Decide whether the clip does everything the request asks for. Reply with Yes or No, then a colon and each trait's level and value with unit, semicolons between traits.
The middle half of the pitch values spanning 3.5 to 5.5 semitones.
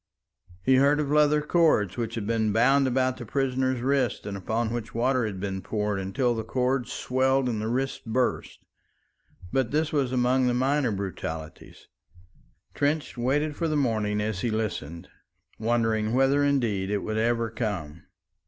Yes: average, 3.8 semitones